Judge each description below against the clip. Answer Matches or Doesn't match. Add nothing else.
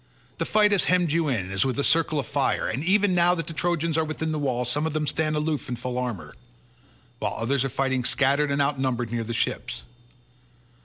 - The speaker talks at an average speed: Doesn't match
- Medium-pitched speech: Matches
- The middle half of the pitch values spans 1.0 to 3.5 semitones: Doesn't match